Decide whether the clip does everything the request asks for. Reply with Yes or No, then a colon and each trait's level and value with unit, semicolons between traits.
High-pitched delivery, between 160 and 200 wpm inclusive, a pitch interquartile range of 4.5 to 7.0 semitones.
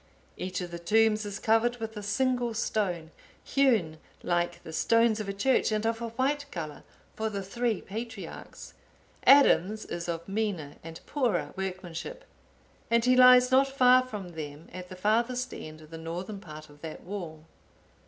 Yes: high, 210 Hz; average, 170 wpm; wide, 5.5 semitones